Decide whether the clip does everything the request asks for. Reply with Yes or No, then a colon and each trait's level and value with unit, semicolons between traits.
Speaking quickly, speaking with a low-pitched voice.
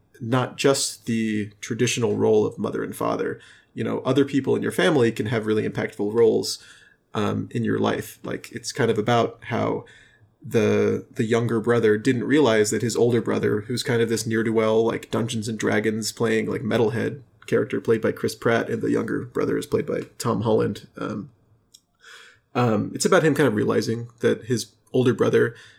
No: average, 190 wpm; low, 115 Hz